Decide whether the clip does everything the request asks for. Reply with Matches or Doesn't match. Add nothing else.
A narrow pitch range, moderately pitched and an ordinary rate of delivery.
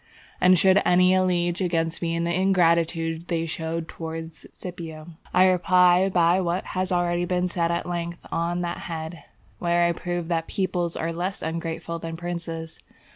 Matches